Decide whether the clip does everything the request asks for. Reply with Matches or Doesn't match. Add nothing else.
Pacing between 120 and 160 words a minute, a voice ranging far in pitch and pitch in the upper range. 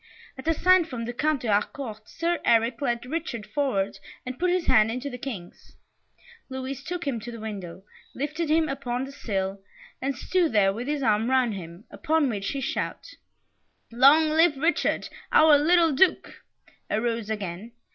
Doesn't match